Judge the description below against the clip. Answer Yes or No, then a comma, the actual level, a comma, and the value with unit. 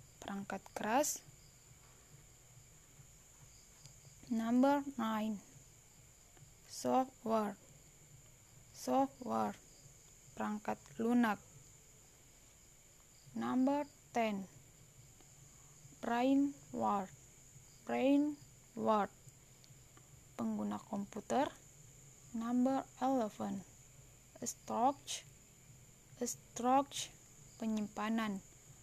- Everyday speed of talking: No, slow, 45 wpm